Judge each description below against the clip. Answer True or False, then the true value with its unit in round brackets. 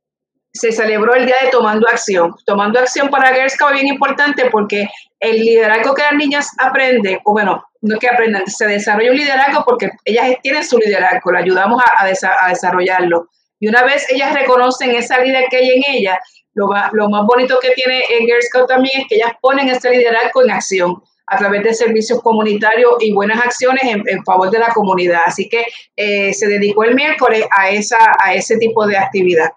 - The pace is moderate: False (205 wpm)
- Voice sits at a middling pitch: False (230 Hz)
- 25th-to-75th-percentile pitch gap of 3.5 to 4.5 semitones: True (3.9 semitones)